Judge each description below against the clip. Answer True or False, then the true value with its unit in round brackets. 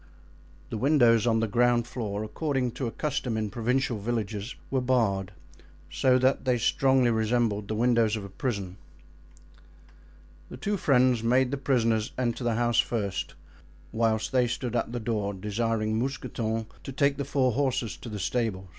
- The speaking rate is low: False (165 wpm)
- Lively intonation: False (2.7 semitones)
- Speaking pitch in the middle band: False (120 Hz)